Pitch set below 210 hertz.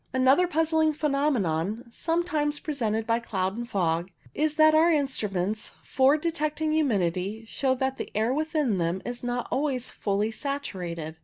No: very high, 255 Hz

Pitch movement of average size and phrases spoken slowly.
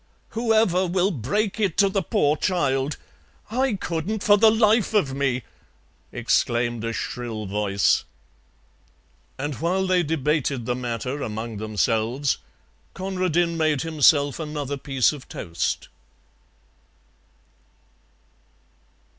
No: wide, 7.2 semitones; slow, 105 wpm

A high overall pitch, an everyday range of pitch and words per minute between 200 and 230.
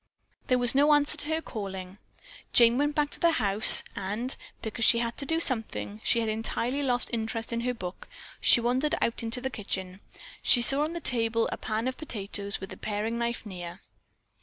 Yes: high, 235 Hz; average, 3.7 semitones; fast, 205 wpm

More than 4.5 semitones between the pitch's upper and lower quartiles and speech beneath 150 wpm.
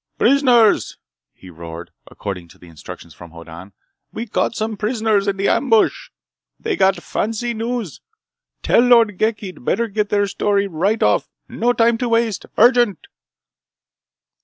Yes: average, 5.1 semitones; average, 140 wpm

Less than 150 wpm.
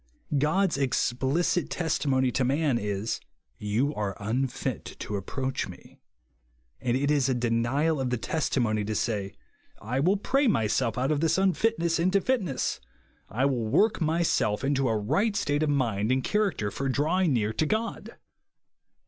No: average, 165 wpm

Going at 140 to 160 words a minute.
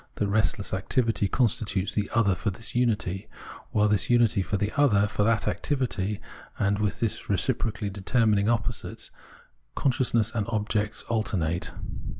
Yes: average, 150 wpm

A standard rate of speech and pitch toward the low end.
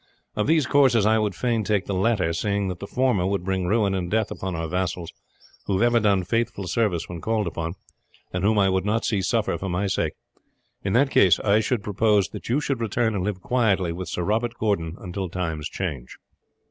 No: fast, 215 wpm; low, 100 Hz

